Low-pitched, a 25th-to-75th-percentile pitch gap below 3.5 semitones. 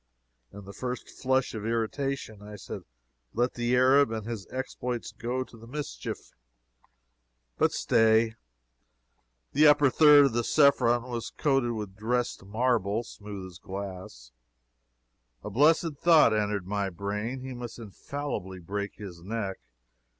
No: low, 115 Hz; average, 4.1 semitones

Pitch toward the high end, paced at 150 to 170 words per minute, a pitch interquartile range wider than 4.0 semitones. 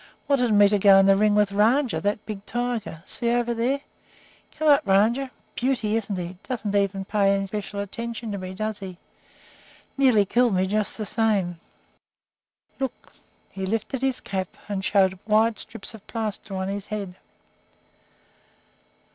No: high, 210 Hz; average, 155 wpm; average, 3.0 semitones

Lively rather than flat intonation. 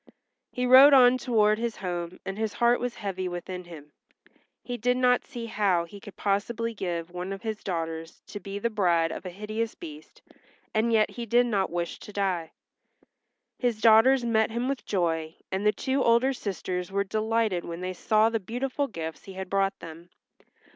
No: average, 4.5 semitones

